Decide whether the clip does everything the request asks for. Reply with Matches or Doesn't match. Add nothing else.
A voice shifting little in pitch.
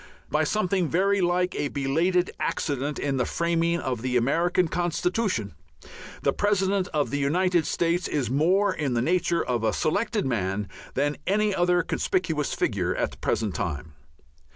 Doesn't match